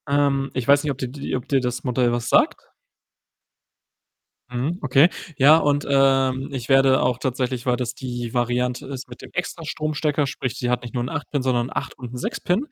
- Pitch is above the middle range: No, low, 130 Hz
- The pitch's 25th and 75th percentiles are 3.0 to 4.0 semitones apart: No, narrow, 2.4 semitones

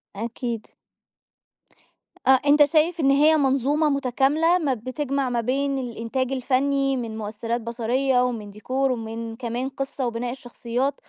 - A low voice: No, very high, 255 Hz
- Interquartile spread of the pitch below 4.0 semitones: Yes, average, 2.9 semitones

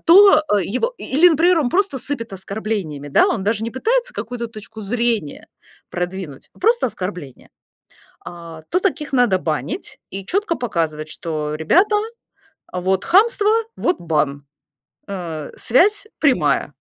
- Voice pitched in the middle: No, high, 220 Hz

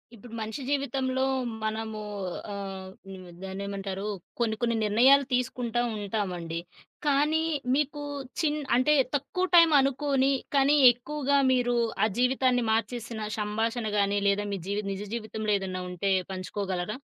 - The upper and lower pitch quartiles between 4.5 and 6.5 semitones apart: Yes, average, 5.0 semitones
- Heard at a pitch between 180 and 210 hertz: No, high, 225 Hz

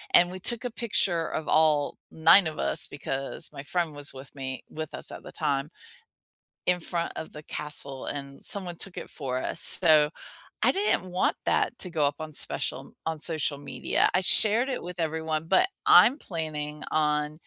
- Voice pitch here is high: No, medium, 155 Hz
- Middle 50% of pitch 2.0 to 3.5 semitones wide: Yes, average, 3.2 semitones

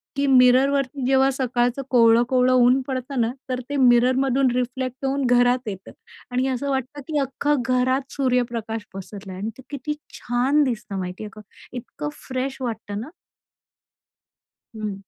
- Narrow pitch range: Yes, narrow, 2.2 semitones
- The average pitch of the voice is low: No, very high, 255 Hz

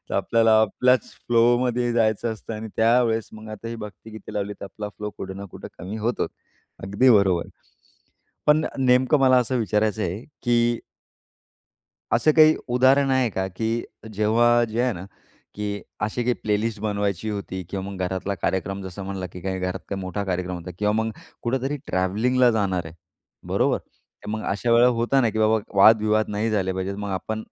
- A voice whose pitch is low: Yes, low, 110 Hz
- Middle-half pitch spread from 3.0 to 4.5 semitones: Yes, average, 3.3 semitones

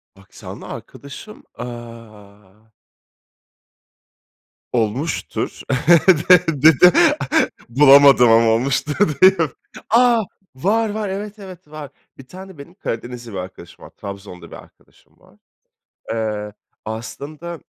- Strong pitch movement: Yes, wide, 8.2 semitones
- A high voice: No, low, 135 Hz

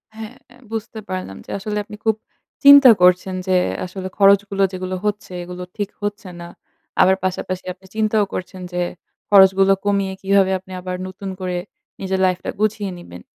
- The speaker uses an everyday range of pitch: No, narrow, 1.9 semitones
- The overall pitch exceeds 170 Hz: Yes, high, 190 Hz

